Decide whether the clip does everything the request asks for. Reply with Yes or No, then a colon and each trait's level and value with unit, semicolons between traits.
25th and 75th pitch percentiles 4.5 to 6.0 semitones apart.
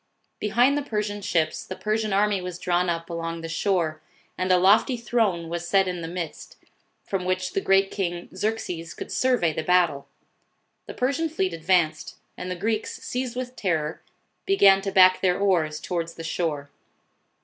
No: average, 3.8 semitones